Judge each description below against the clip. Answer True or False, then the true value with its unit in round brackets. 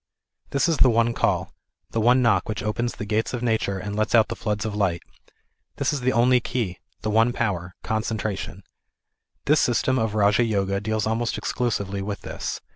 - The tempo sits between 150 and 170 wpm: False (195 wpm)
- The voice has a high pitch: False (110 Hz)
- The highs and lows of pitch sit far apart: False (2.8 semitones)